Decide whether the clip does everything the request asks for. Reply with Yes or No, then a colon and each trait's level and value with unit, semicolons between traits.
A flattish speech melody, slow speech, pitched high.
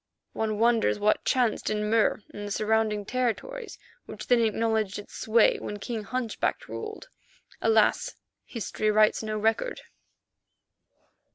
Yes: narrow, 2.0 semitones; slow, 125 wpm; high, 220 Hz